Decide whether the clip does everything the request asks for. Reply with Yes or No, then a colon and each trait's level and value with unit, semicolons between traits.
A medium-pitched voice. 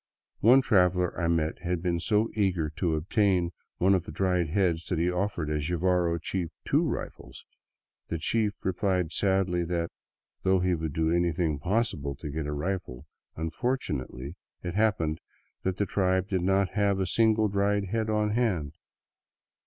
No: very low, 90 Hz